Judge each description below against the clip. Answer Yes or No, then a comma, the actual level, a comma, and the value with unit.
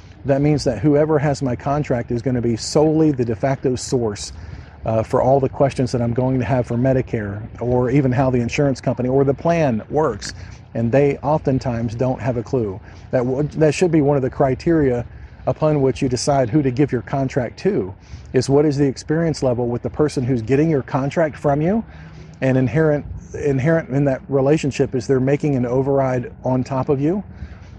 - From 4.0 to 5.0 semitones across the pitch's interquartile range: No, average, 2.9 semitones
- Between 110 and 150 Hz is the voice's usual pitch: Yes, low, 130 Hz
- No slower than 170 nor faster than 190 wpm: No, fast, 205 wpm